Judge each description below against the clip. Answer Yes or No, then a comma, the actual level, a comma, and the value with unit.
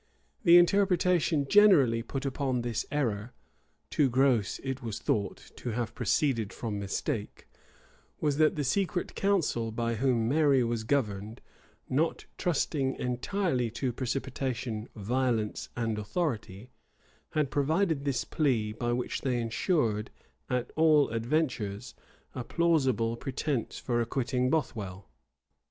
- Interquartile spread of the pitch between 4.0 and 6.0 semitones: Yes, average, 4.4 semitones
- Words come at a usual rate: No, slow, 125 wpm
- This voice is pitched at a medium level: No, low, 125 Hz